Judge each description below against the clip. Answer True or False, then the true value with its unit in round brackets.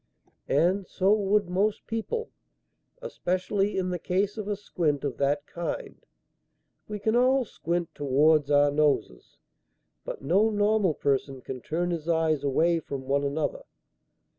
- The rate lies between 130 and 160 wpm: True (140 wpm)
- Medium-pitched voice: True (175 Hz)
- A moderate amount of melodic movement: False (6.0 semitones)